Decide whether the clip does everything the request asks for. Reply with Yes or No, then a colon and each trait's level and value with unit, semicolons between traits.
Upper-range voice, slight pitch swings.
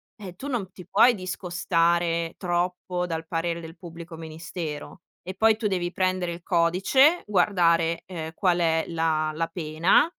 No: medium, 175 Hz; narrow, 2.0 semitones